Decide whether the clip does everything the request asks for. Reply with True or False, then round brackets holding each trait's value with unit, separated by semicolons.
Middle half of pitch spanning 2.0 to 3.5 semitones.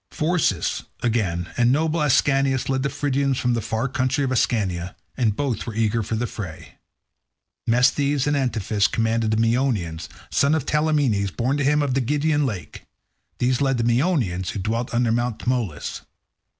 False (4.1 semitones)